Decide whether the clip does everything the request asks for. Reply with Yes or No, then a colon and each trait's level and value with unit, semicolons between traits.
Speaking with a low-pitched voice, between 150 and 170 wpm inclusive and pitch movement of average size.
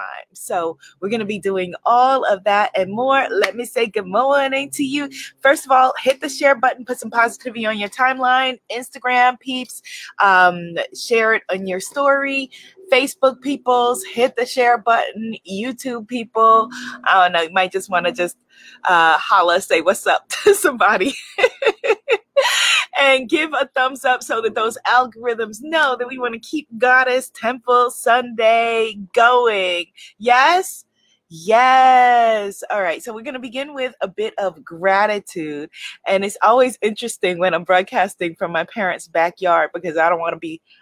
No: high, 240 Hz; average, 165 wpm; average, 4.7 semitones